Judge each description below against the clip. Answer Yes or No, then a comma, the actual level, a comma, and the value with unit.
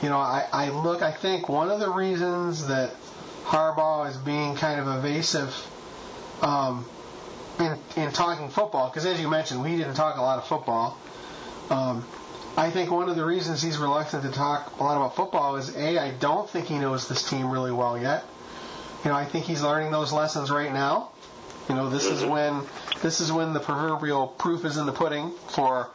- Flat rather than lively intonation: No, average, 3.0 semitones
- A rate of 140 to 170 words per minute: No, average, 200 wpm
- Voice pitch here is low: No, medium, 150 Hz